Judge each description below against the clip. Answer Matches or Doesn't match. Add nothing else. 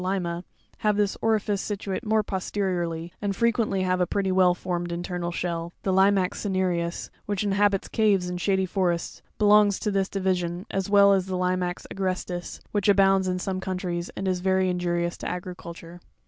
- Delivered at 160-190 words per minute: Matches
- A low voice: Doesn't match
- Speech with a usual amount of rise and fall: Doesn't match